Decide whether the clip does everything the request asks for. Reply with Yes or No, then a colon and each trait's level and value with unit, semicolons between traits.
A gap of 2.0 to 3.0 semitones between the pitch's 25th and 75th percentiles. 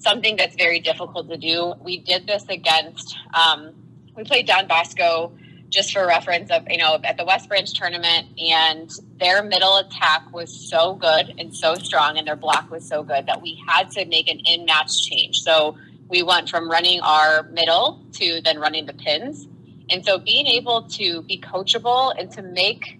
Yes: narrow, 2.5 semitones